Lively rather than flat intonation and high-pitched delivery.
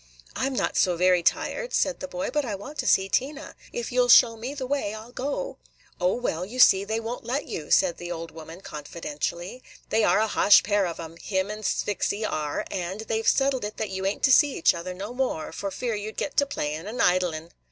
Yes: wide, 5.9 semitones; high, 210 Hz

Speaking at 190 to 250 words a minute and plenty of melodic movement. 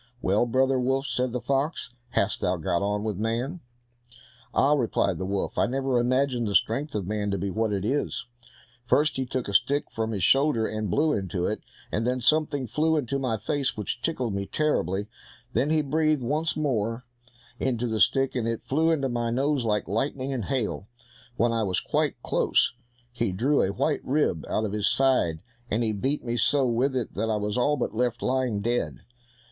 No: average, 200 wpm; average, 4.3 semitones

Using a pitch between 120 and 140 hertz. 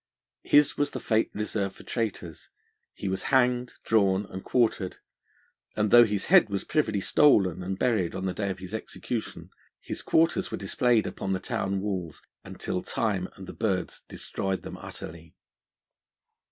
No: low, 100 Hz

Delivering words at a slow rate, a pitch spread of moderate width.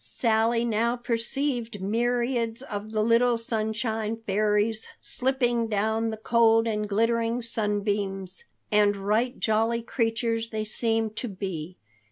No: slow, 120 wpm; narrow, 1.7 semitones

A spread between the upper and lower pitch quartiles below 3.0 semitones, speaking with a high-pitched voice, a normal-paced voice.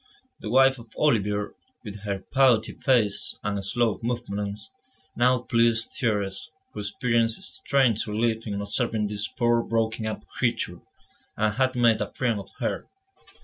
No: narrow, 2.6 semitones; low, 115 Hz; average, 145 wpm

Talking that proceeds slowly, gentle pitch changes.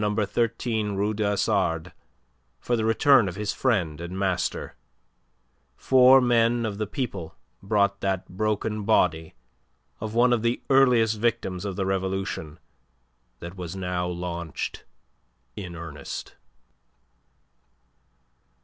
No: slow, 115 wpm; average, 3.8 semitones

